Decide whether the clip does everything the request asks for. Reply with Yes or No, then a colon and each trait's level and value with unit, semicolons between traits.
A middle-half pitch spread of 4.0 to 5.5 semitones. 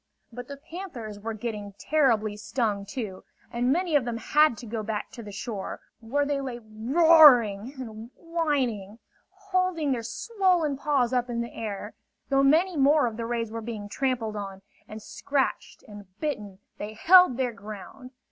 Yes: average, 5.1 semitones